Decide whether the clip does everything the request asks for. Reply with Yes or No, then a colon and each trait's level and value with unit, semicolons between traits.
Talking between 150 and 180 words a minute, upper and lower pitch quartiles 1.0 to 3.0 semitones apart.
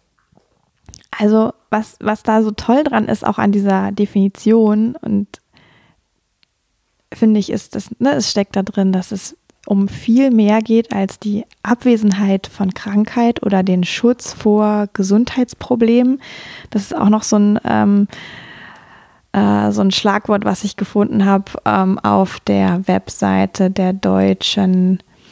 No: average, 140 wpm; narrow, 2.6 semitones